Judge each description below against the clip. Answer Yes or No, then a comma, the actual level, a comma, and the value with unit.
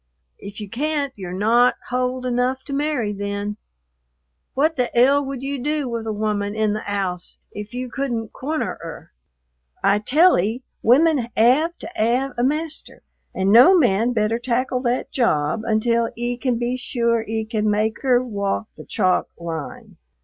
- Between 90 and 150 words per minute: No, average, 165 wpm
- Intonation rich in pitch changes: No, average, 3.7 semitones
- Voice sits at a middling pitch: No, high, 235 Hz